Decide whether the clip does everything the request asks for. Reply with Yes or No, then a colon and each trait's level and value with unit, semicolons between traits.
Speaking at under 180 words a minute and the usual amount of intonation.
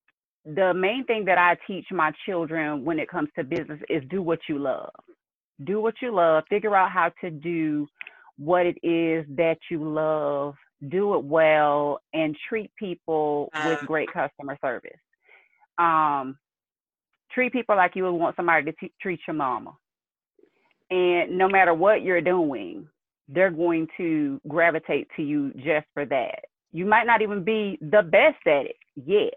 No: average, 165 wpm; wide, 5.9 semitones